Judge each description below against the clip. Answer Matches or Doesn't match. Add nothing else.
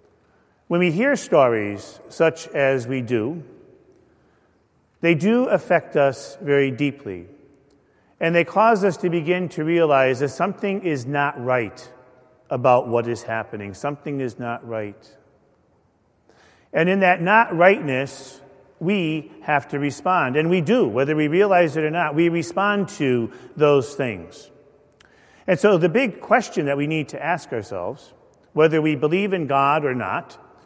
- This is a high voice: Doesn't match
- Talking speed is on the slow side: Doesn't match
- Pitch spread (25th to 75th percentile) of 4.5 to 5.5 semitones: Matches